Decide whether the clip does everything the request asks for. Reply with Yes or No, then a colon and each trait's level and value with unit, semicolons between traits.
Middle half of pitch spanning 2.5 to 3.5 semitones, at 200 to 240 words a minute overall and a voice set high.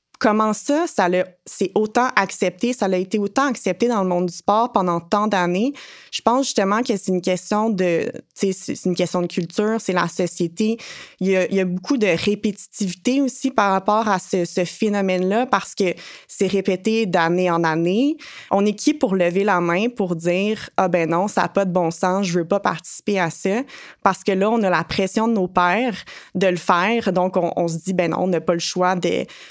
Yes: average, 3.2 semitones; fast, 220 wpm; high, 195 Hz